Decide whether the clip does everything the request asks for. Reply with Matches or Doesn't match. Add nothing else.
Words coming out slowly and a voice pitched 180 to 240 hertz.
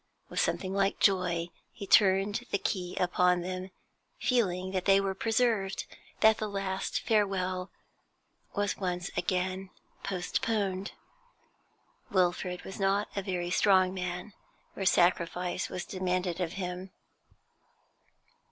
Matches